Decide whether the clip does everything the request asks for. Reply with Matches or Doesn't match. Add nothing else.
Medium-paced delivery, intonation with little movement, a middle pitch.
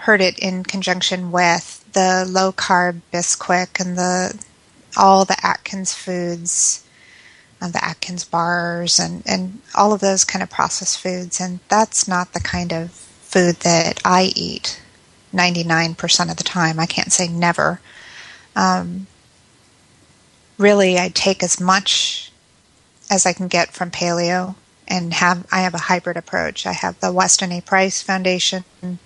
Matches